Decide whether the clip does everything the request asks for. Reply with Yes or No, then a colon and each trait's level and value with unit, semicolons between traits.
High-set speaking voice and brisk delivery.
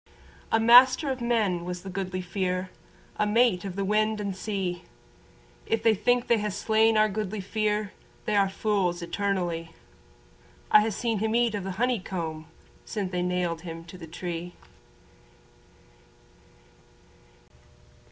No: high, 200 Hz; average, 145 wpm